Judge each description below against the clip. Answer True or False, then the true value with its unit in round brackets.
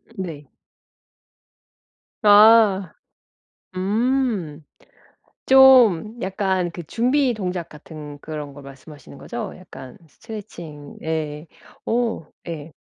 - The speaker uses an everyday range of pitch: False (6.6 semitones)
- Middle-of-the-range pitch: True (180 Hz)